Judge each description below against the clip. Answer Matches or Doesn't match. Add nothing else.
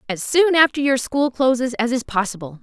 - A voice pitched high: Matches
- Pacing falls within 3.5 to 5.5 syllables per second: Matches